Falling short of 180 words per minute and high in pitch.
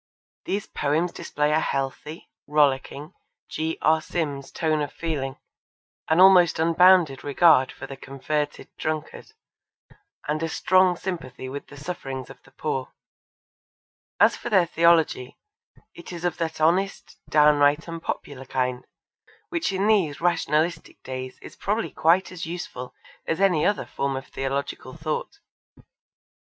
No: slow, 135 wpm; medium, 155 Hz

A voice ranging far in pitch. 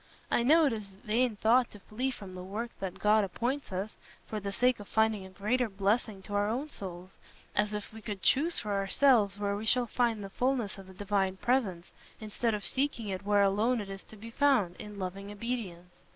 No: average, 3.3 semitones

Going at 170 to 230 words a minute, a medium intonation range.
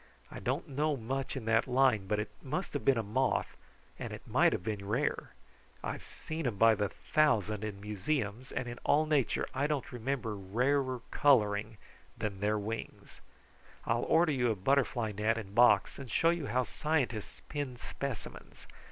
Yes: average, 175 wpm; average, 4.6 semitones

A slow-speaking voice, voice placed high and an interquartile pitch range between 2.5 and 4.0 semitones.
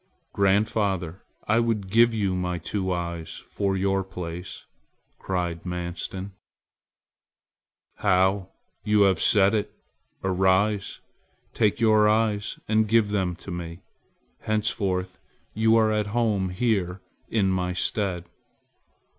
No: slow, 115 wpm; very low, 95 Hz; average, 2.8 semitones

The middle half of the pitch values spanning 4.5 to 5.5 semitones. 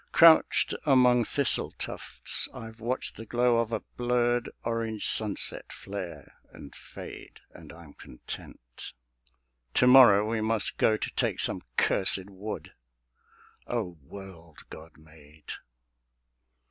Yes: average, 5.2 semitones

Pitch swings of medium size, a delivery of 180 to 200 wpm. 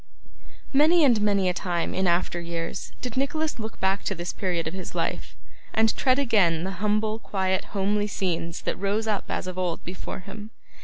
Yes: average, 3.4 semitones; average, 190 wpm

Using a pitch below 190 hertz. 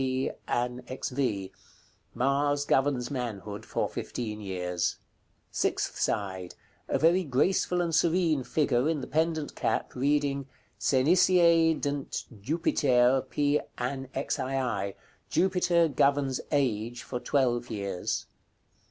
Yes: low, 135 Hz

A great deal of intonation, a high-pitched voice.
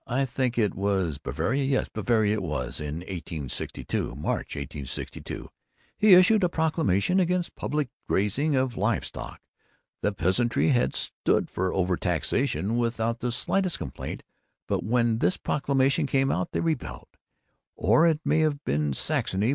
No: wide, 7.2 semitones; low, 120 Hz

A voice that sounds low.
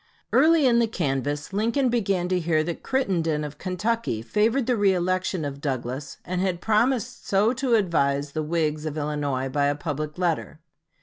No: medium, 175 Hz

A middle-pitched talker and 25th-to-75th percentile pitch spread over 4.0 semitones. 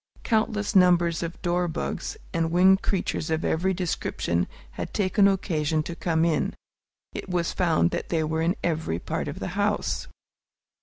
No: medium, 170 Hz; narrow, 2.6 semitones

